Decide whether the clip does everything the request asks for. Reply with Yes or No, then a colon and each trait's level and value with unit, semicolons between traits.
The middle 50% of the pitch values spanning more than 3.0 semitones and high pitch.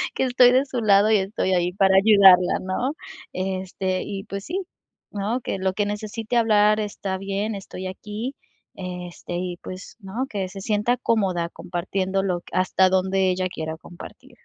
No: narrow, 2.4 semitones; high, 195 Hz